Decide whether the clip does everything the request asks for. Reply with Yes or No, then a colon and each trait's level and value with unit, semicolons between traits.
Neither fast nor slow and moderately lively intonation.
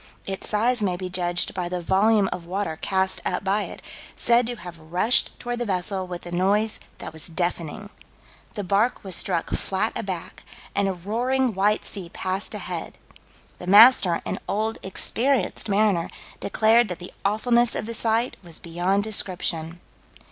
Yes: average, 165 wpm; average, 3.6 semitones